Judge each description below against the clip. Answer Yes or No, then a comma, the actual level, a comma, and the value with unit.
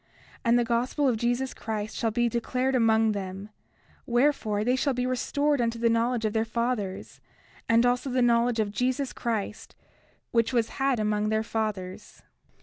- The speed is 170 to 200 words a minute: Yes, average, 175 wpm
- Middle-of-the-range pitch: No, high, 235 Hz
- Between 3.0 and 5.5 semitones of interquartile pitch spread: No, narrow, 2.4 semitones